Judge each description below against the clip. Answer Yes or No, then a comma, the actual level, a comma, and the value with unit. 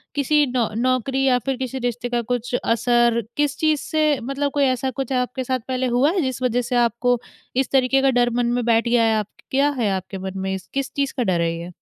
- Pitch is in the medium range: No, very high, 250 Hz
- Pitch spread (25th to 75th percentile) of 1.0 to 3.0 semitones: Yes, narrow, 2.4 semitones